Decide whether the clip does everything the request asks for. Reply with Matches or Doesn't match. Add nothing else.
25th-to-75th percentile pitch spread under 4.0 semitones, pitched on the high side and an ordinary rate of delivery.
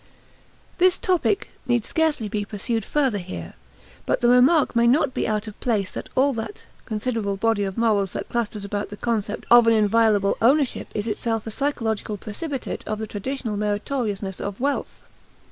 Matches